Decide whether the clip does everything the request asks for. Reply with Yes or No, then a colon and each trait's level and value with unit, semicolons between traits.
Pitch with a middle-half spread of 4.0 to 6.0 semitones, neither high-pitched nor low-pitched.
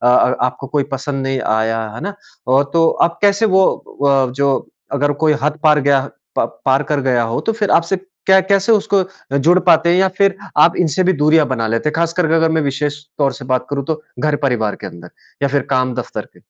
Yes: average, 4.3 semitones; medium, 145 Hz